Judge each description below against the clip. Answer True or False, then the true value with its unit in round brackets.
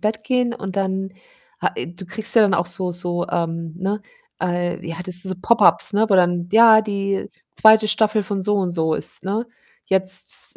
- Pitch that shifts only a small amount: False (3.3 semitones)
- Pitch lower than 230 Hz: True (190 Hz)